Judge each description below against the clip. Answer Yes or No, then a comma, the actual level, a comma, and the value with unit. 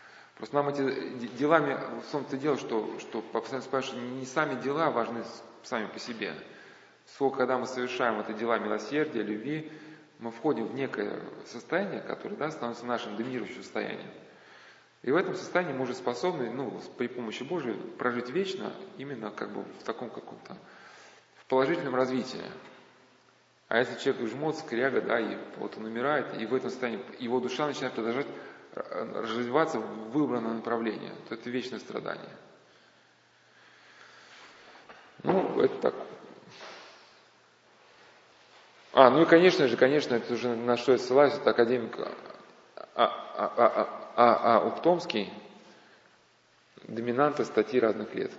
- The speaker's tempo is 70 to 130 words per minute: No, average, 140 wpm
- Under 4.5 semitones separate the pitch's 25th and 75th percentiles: Yes, average, 4.1 semitones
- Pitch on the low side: Yes, low, 130 Hz